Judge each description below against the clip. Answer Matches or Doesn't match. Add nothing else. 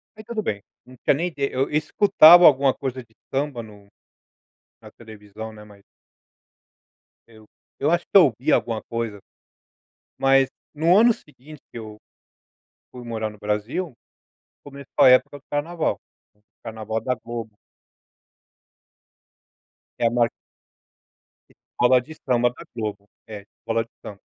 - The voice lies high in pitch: Doesn't match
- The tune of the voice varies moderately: Matches